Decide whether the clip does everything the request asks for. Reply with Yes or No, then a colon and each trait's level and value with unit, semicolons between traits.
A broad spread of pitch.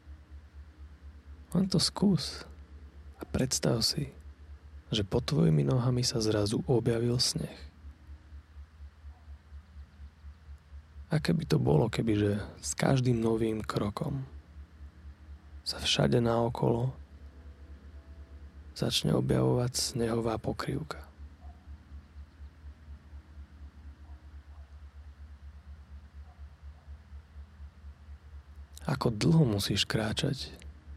Yes: wide, 6.7 semitones